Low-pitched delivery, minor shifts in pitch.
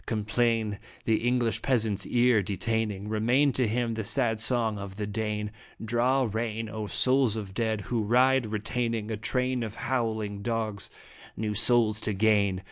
Yes: low, 110 Hz; narrow, 2.2 semitones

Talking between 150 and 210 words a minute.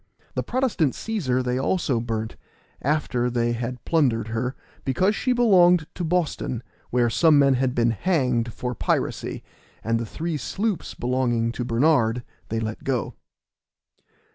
No: average, 140 wpm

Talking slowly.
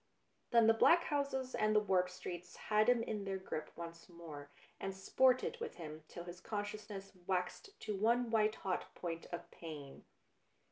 No: average, 170 wpm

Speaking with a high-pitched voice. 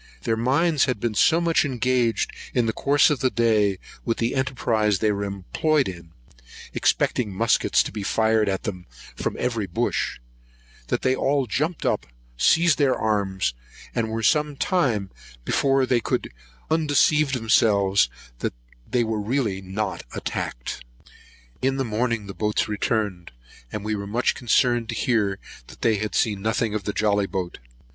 No: low, 115 Hz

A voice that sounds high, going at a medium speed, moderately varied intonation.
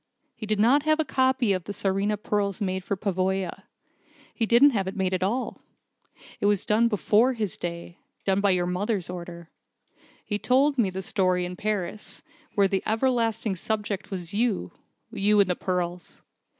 Yes: high, 200 Hz; average, 175 wpm; average, 3.2 semitones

